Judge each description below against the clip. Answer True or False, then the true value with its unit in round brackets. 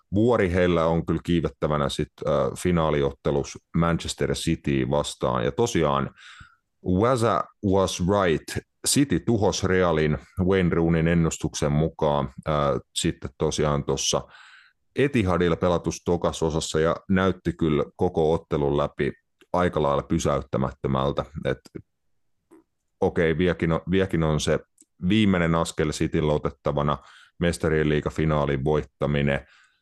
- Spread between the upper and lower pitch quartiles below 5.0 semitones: True (3.0 semitones)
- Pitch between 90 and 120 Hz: False (80 Hz)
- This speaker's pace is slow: False (105 wpm)